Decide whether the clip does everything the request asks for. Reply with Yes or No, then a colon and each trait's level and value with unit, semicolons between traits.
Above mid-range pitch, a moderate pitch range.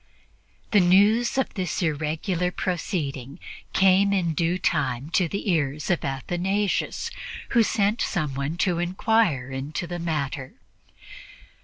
No: medium, 175 Hz; average, 4.6 semitones